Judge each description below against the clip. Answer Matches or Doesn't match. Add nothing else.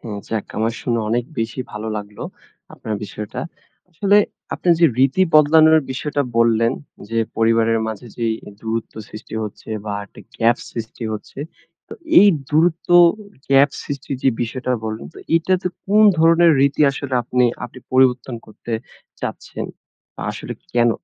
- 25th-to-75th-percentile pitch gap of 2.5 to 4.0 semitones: Doesn't match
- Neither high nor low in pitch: Doesn't match